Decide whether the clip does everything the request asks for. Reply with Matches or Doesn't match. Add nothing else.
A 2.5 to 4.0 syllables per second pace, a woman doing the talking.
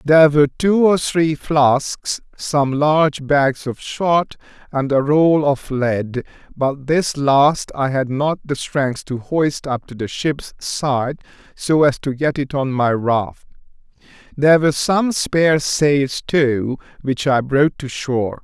Doesn't match